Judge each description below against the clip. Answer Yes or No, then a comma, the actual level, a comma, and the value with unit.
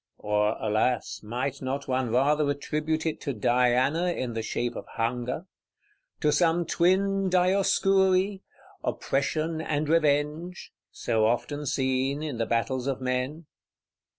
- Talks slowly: Yes, slow, 125 wpm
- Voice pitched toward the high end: No, medium, 140 Hz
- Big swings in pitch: No, average, 4.7 semitones